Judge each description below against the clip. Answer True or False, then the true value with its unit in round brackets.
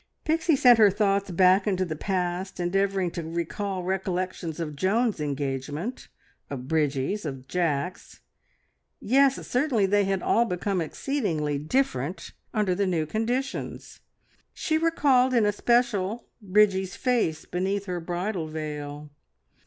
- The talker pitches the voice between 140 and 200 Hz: True (190 Hz)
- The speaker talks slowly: True (125 wpm)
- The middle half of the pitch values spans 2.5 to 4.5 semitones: False (5.0 semitones)